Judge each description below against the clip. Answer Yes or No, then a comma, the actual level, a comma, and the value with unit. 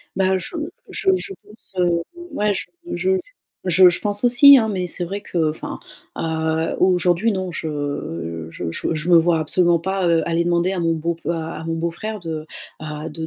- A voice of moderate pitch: Yes, medium, 170 Hz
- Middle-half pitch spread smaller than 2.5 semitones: No, average, 2.8 semitones